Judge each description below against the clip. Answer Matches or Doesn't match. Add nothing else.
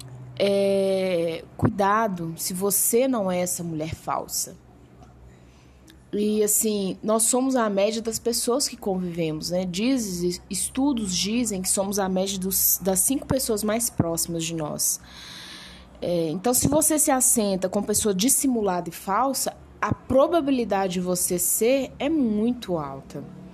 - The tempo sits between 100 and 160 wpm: Matches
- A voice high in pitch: Matches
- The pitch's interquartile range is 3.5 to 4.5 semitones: Doesn't match